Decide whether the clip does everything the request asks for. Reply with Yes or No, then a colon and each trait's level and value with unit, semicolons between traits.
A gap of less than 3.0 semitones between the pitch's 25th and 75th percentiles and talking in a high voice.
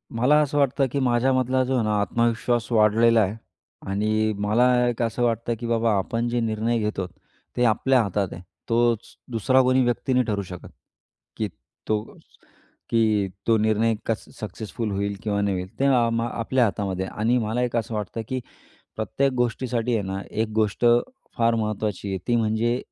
No: narrow, 2.4 semitones; low, 115 Hz